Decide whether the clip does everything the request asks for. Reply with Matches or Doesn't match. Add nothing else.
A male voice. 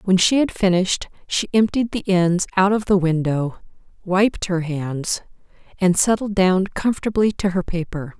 Doesn't match